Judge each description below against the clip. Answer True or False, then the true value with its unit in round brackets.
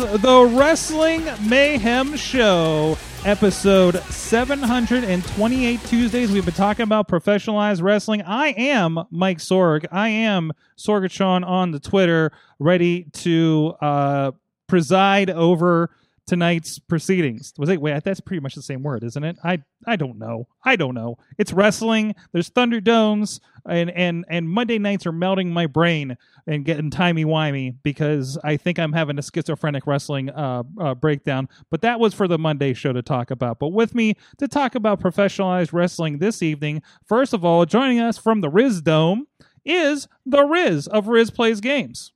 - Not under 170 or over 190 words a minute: False (160 wpm)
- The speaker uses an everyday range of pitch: False (6.1 semitones)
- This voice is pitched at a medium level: True (180 Hz)